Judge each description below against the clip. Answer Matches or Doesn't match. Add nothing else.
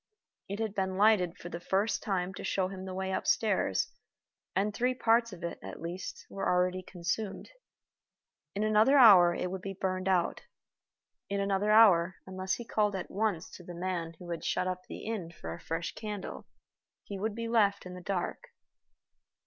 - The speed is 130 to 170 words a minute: Doesn't match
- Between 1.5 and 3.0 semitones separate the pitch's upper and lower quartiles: Matches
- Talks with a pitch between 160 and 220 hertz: Matches